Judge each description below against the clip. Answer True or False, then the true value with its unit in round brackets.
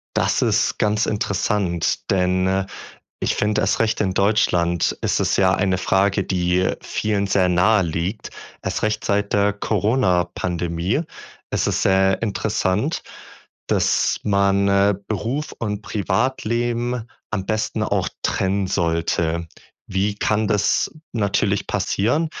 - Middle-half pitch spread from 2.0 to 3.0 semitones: True (2.5 semitones)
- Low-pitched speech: True (100 Hz)